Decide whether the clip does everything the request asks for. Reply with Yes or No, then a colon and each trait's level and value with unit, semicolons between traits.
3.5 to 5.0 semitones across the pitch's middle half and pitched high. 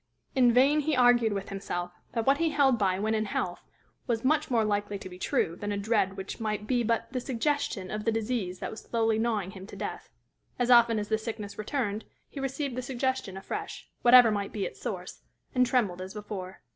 Yes: average, 3.8 semitones; high, 225 Hz